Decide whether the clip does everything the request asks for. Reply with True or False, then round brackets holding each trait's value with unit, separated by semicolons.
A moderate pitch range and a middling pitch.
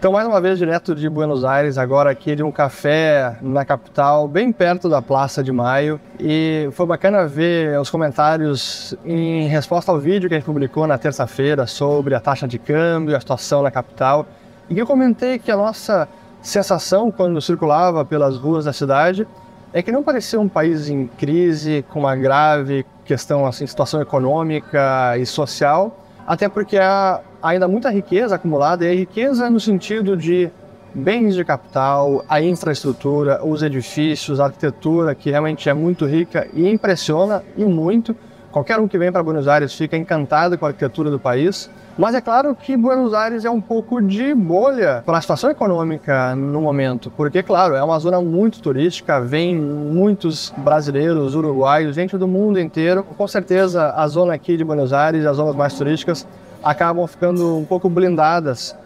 True (4.5 semitones; 160 Hz)